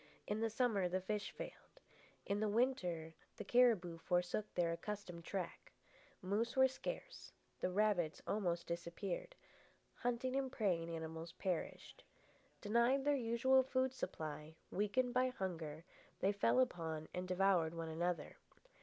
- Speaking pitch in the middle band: No, high, 195 Hz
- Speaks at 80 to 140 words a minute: Yes, slow, 135 wpm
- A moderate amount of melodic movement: No, wide, 5.8 semitones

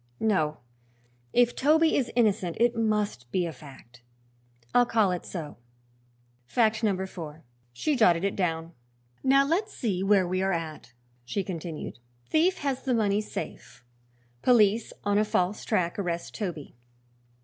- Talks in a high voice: Yes, high, 200 Hz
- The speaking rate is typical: Yes, average, 145 wpm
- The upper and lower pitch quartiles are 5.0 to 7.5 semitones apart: Yes, wide, 5.6 semitones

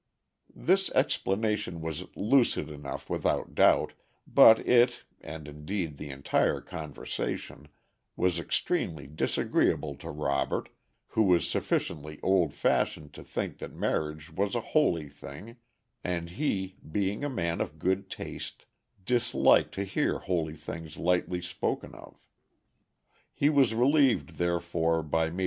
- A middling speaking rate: No, slow, 125 wpm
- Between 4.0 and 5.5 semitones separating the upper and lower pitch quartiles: Yes, average, 5.0 semitones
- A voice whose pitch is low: Yes, very low, 85 Hz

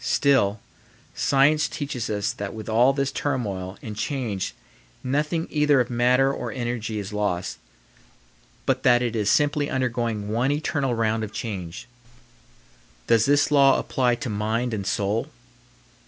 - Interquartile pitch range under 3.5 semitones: No, average, 4.4 semitones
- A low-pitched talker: Yes, low, 120 Hz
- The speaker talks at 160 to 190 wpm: No, average, 140 wpm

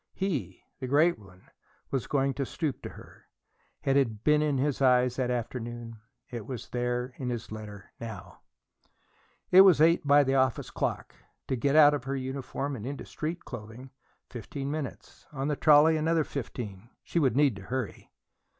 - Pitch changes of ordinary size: Yes, average, 3.5 semitones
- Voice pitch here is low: Yes, low, 130 Hz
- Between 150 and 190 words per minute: Yes, average, 175 wpm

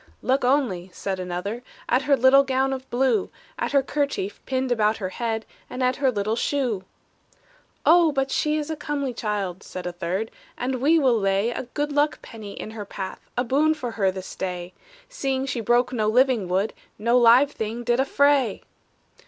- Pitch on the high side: Yes, high, 245 Hz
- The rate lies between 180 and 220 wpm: Yes, average, 185 wpm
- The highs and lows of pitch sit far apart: No, average, 4.6 semitones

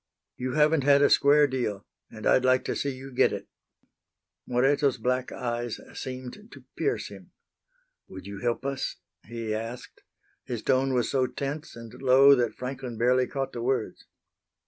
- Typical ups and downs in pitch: No, narrow, 2.3 semitones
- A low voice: Yes, low, 130 Hz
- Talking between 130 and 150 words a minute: No, average, 165 wpm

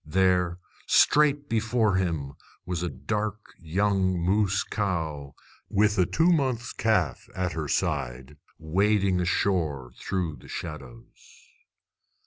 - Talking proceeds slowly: Yes, slow, 110 wpm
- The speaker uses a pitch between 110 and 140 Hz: No, very low, 95 Hz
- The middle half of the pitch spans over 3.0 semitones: Yes, average, 4.8 semitones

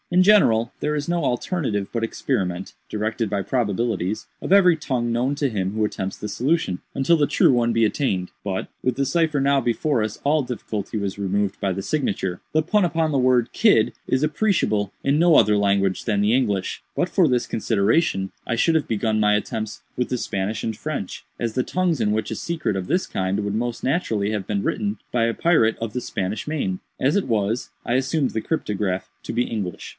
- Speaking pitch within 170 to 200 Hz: No, low, 115 Hz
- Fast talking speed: Yes, fast, 210 wpm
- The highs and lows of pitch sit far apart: Yes, wide, 6.1 semitones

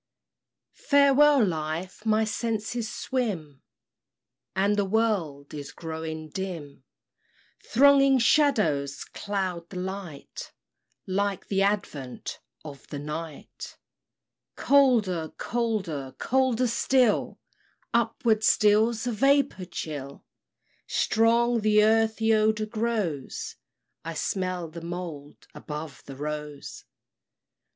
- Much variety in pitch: Yes, wide, 6.2 semitones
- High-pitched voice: Yes, high, 200 Hz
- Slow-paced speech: Yes, slow, 95 wpm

